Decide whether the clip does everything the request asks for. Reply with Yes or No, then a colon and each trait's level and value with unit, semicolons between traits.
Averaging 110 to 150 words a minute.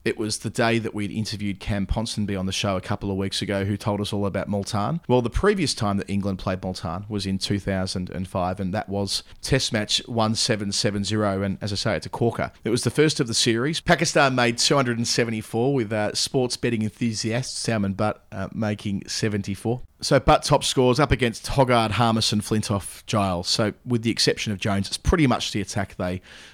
No: average, 200 wpm